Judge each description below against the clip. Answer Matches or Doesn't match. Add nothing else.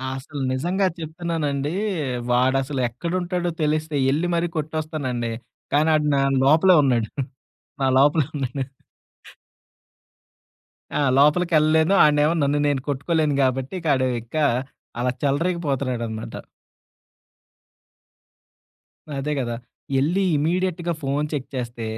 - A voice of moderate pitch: Matches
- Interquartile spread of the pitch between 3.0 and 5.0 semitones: Matches